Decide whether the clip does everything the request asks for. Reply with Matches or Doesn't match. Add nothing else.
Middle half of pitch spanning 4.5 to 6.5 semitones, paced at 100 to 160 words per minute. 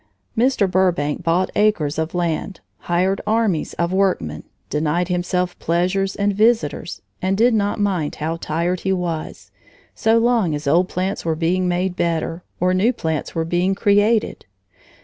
Doesn't match